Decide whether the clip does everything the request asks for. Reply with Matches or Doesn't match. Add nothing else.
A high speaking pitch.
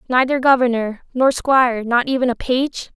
Matches